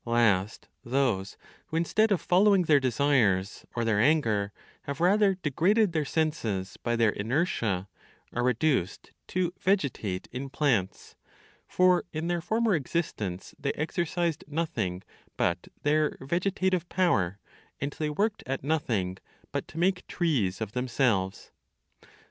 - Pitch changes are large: Yes, wide, 8.0 semitones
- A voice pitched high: No, medium, 140 Hz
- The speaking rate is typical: No, slow, 130 wpm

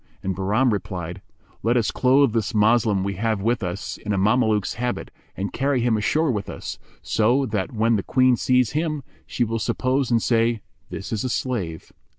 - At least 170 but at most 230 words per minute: Yes, average, 185 wpm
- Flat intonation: No, average, 3.8 semitones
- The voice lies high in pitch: No, low, 115 Hz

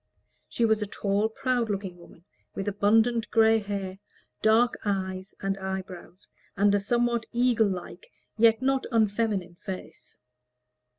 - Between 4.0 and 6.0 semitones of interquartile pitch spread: No, average, 3.0 semitones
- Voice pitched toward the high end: Yes, high, 205 Hz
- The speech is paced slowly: Yes, slow, 130 wpm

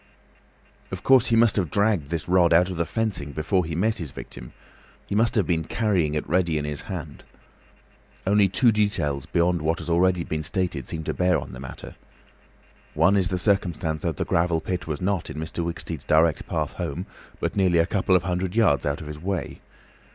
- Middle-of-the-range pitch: No, very low, 85 Hz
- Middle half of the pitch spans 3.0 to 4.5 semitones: Yes, average, 3.6 semitones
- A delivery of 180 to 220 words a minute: Yes, fast, 205 wpm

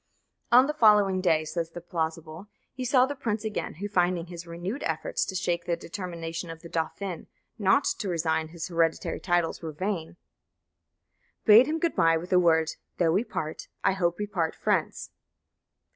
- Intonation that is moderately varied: Yes, average, 3.9 semitones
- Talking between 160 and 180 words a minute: Yes, average, 175 wpm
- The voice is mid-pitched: Yes, medium, 175 Hz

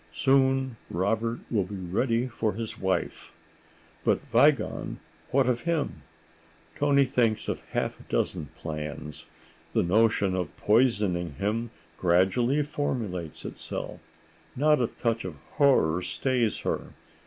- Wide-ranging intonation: Yes, wide, 6.0 semitones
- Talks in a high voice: No, low, 115 Hz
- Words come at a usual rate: No, slow, 120 wpm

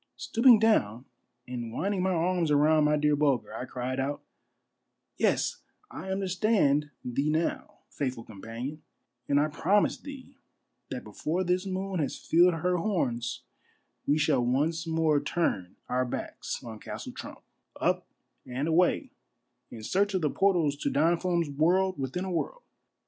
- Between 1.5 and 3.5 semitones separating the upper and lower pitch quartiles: No, wide, 5.4 semitones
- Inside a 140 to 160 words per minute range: Yes, average, 155 wpm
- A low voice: No, medium, 155 Hz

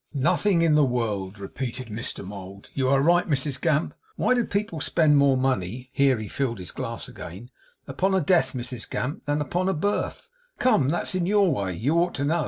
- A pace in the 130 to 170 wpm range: No, average, 200 wpm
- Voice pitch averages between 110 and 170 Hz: Yes, medium, 140 Hz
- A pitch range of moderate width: No, wide, 6.1 semitones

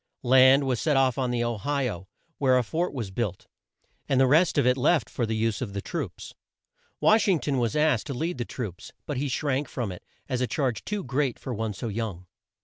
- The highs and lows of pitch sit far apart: No, average, 3.8 semitones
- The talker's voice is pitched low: Yes, low, 125 Hz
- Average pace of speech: No, fast, 235 wpm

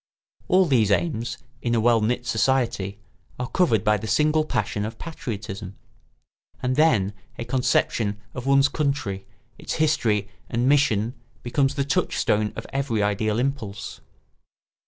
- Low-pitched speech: Yes, low, 120 Hz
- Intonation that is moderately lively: Yes, average, 4.7 semitones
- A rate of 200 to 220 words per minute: No, slow, 135 wpm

